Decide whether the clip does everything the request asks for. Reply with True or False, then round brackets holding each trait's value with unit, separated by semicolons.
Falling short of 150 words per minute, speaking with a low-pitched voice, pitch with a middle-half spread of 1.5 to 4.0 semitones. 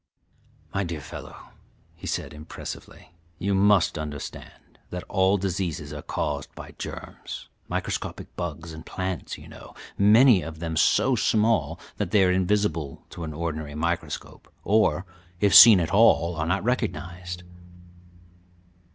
True (140 wpm; 90 Hz; 3.6 semitones)